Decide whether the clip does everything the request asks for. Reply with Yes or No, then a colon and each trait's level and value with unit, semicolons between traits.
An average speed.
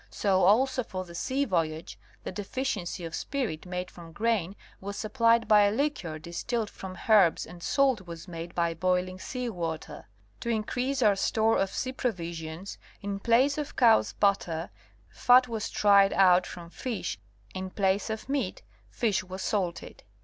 Yes: average, 160 wpm